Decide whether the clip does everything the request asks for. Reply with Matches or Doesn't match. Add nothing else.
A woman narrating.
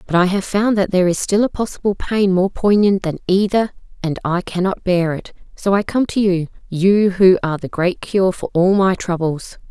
Matches